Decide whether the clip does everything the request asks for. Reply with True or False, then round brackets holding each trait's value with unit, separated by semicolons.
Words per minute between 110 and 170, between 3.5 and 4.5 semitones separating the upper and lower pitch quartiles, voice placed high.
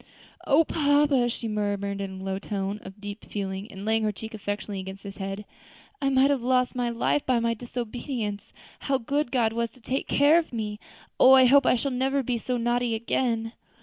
False (200 wpm; 4.0 semitones; 230 Hz)